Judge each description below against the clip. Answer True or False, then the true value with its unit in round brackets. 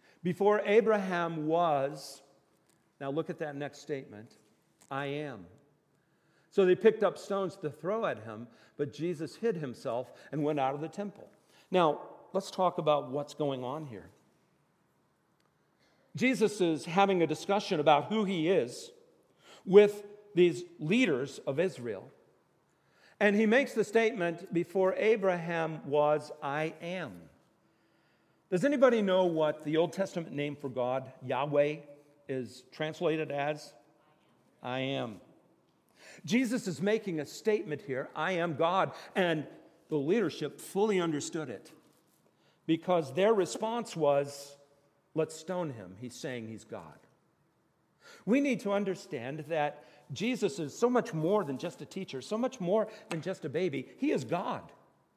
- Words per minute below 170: True (140 wpm)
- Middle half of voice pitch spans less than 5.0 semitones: False (5.4 semitones)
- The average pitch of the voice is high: False (165 Hz)